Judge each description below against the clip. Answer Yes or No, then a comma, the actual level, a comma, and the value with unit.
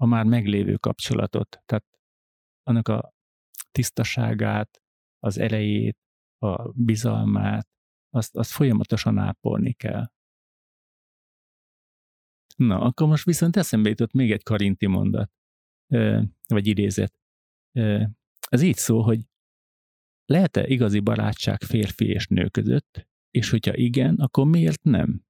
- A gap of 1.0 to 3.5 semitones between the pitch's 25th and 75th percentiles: Yes, narrow, 2.6 semitones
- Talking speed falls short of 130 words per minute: Yes, average, 110 wpm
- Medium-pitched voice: No, low, 110 Hz